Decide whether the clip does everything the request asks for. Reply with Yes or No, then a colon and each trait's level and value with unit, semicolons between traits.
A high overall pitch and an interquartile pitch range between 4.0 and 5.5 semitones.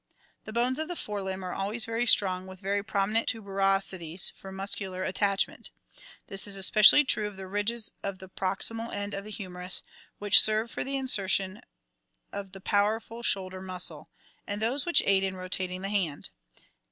No: high, 195 Hz; narrow, 2.4 semitones